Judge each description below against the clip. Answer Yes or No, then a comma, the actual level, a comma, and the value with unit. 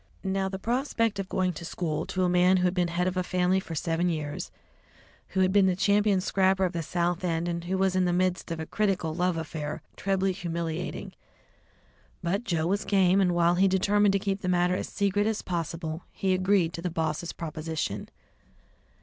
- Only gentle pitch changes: Yes, narrow, 2.2 semitones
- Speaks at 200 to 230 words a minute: Yes, fast, 205 wpm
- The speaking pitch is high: No, medium, 180 Hz